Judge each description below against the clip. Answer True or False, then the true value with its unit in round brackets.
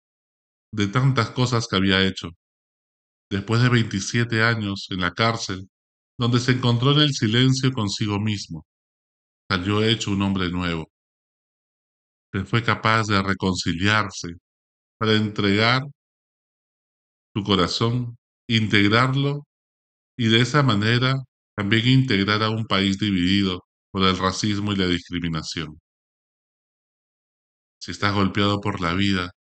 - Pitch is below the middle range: True (100 Hz)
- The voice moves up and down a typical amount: True (4.3 semitones)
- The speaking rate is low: True (120 wpm)